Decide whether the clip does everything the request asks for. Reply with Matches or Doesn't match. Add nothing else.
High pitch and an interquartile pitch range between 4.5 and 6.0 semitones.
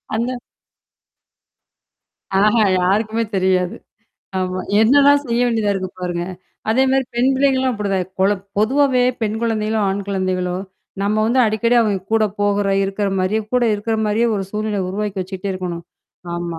Doesn't match